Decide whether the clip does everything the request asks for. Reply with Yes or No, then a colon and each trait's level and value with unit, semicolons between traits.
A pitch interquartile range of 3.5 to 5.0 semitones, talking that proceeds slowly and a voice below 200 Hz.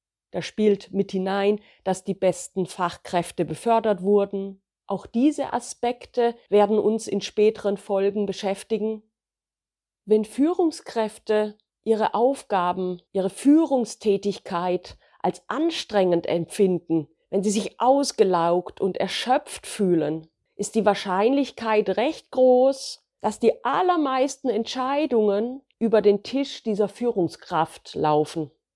No: average, 3.8 semitones; slow, 105 wpm; high, 210 Hz